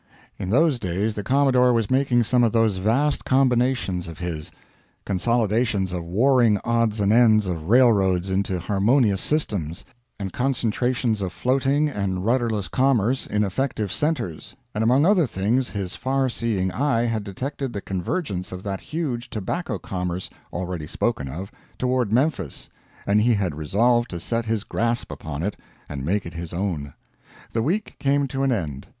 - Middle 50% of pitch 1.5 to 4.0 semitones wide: No, average, 5.2 semitones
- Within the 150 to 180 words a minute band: Yes, average, 160 wpm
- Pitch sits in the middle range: No, low, 110 Hz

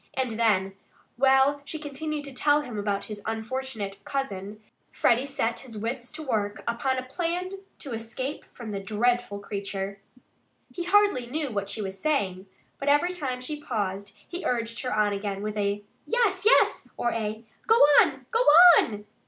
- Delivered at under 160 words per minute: No, average, 170 wpm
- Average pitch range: No, wide, 5.9 semitones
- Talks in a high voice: Yes, high, 240 Hz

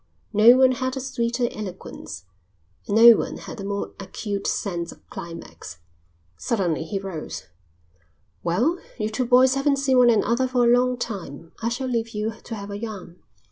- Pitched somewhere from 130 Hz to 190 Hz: No, high, 225 Hz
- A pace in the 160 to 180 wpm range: Yes, average, 175 wpm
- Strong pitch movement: No, average, 4.2 semitones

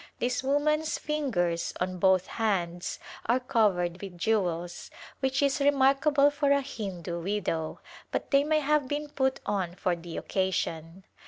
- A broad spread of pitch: Yes, wide, 7.9 semitones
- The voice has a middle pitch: No, high, 215 Hz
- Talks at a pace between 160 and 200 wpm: No, average, 145 wpm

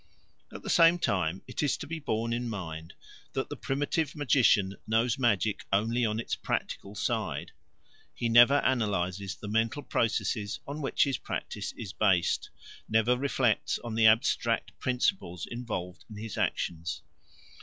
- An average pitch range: Yes, average, 3.9 semitones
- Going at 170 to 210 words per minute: No, average, 150 wpm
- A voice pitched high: No, low, 115 Hz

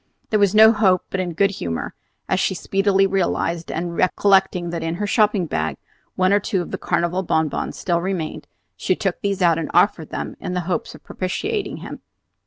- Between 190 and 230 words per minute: Yes, average, 195 wpm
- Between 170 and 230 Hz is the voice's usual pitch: Yes, medium, 185 Hz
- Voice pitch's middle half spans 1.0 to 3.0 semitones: Yes, narrow, 2.6 semitones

